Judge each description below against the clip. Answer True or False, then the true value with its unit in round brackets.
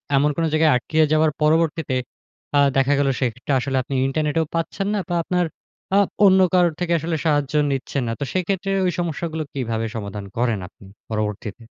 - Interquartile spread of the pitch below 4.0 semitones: False (4.8 semitones)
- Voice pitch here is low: False (150 Hz)